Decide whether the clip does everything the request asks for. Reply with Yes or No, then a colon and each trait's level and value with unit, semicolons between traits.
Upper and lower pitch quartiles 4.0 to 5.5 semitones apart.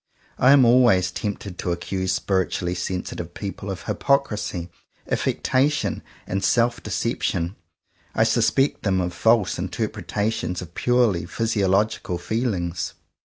Yes: average, 4.4 semitones